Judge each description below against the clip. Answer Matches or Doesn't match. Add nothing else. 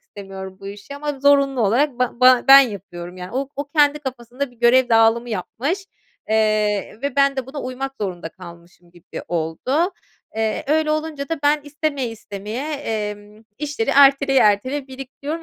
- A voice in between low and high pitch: Doesn't match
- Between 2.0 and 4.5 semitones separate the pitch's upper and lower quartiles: Doesn't match